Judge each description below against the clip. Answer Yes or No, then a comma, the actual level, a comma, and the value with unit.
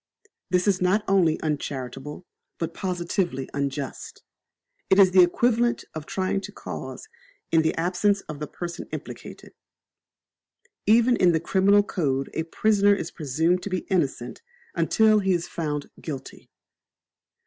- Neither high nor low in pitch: Yes, medium, 175 Hz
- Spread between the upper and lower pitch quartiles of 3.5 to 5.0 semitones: Yes, average, 4.4 semitones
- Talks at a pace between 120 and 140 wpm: Yes, slow, 135 wpm